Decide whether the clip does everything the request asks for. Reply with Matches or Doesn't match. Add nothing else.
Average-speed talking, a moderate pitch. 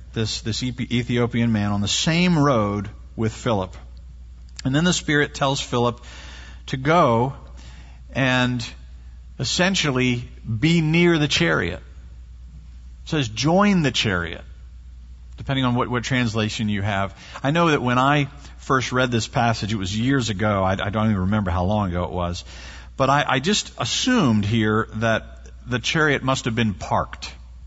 Doesn't match